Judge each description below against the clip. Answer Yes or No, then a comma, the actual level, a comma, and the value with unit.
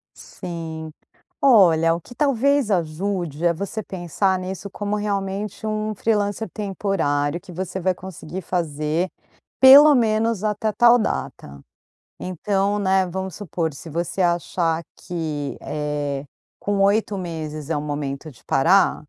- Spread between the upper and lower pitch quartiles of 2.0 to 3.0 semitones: No, average, 4.3 semitones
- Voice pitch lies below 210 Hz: Yes, medium, 185 Hz